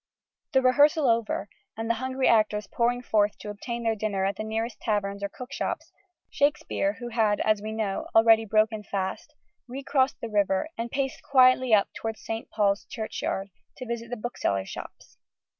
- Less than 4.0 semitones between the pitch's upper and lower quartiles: Yes, average, 3.2 semitones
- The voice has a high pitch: Yes, high, 225 Hz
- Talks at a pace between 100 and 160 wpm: No, average, 175 wpm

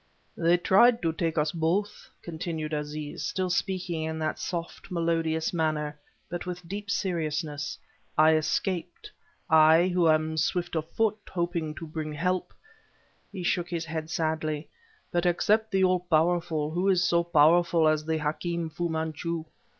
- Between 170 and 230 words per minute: No, average, 150 wpm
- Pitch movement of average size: No, narrow, 2.1 semitones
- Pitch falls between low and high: Yes, medium, 165 Hz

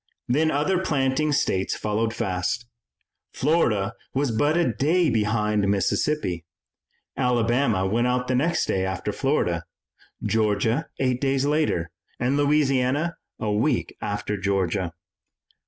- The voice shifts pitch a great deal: Yes, wide, 5.9 semitones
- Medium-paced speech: No, slow, 120 wpm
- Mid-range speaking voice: No, low, 120 Hz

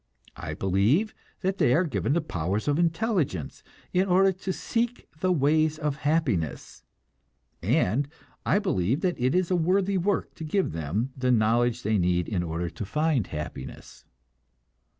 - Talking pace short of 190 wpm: Yes, average, 155 wpm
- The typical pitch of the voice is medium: Yes, medium, 145 Hz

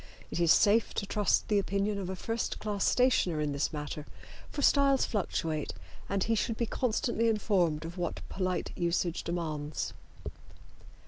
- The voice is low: No, high, 195 Hz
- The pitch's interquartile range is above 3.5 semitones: Yes, average, 4.7 semitones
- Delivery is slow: No, average, 155 wpm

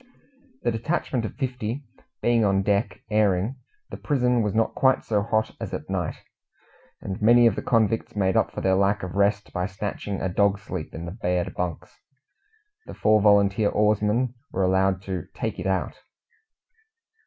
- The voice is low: Yes, low, 100 Hz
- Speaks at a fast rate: No, average, 170 wpm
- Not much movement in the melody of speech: No, average, 3.0 semitones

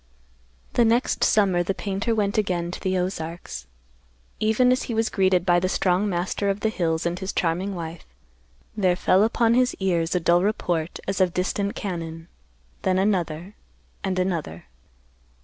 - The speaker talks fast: No, average, 165 wpm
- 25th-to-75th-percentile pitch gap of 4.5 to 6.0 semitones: No, average, 2.8 semitones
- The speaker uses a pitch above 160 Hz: Yes, medium, 185 Hz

